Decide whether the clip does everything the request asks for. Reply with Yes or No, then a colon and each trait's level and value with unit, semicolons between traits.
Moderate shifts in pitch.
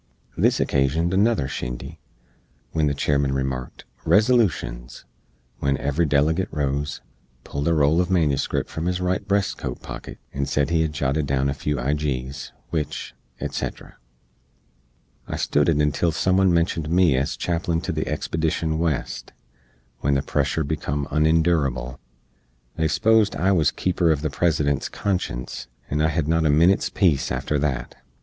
Yes: average, 3.4 semitones